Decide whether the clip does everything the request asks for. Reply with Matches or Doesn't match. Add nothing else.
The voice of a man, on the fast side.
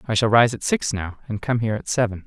Matches